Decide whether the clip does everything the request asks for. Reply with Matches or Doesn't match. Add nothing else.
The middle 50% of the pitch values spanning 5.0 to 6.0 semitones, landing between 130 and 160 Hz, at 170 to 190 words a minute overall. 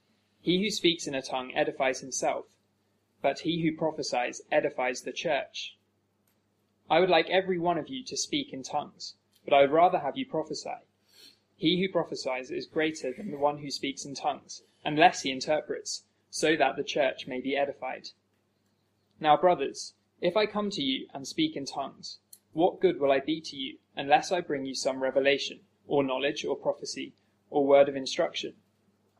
Matches